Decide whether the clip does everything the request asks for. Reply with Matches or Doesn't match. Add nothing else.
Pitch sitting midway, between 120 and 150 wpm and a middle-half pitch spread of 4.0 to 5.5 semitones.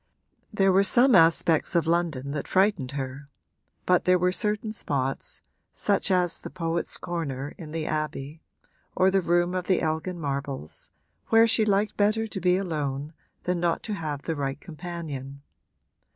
Doesn't match